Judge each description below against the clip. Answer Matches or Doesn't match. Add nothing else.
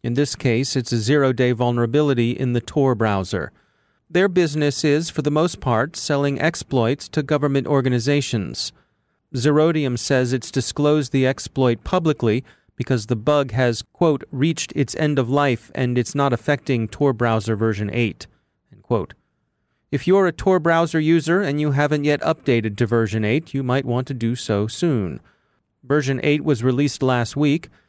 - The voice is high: Doesn't match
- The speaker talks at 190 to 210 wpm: Doesn't match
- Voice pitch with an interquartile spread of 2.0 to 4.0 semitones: Matches